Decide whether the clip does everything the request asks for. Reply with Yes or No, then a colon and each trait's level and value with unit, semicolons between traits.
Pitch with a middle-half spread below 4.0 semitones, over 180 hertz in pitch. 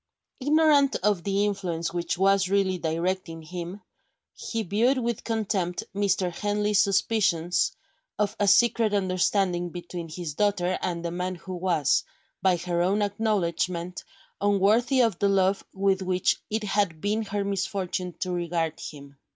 Yes: average, 2.8 semitones; high, 190 Hz